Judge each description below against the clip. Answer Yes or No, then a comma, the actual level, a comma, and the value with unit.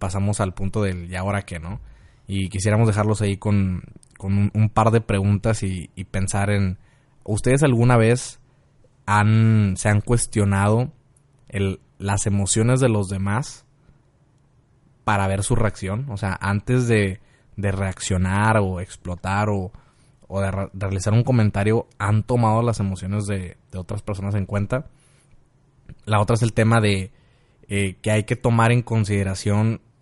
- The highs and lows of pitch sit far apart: No, average, 3.7 semitones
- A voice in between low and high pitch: No, low, 105 Hz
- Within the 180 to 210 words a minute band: No, average, 155 wpm